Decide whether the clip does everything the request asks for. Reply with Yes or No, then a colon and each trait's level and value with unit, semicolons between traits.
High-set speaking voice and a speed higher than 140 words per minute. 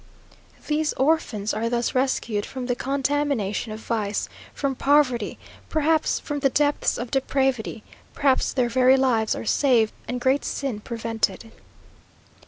No: very high, 255 Hz; slow, 135 wpm